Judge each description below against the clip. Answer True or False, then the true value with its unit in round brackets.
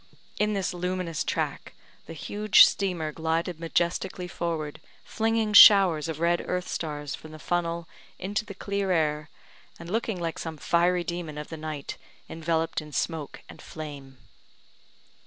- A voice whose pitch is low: False (170 Hz)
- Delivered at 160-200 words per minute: False (145 wpm)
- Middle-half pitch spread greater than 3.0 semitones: False (2.7 semitones)